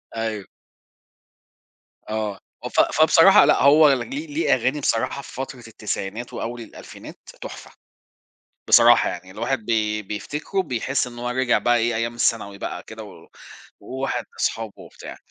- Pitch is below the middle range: Yes, low, 120 Hz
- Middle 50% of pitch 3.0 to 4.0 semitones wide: Yes, average, 3.3 semitones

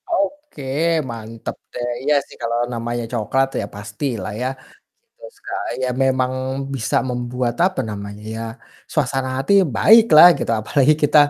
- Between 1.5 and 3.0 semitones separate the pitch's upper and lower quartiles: No, average, 4.2 semitones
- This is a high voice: No, low, 130 Hz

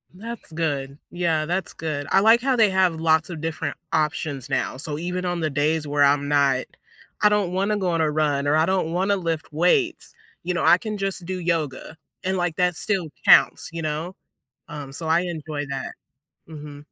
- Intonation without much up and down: No, average, 3.5 semitones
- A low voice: No, medium, 160 Hz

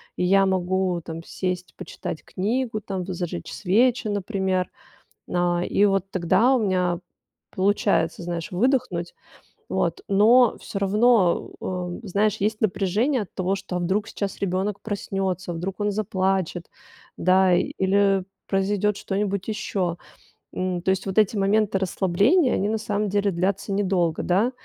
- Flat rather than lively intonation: Yes, narrow, 2.2 semitones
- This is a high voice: Yes, high, 195 Hz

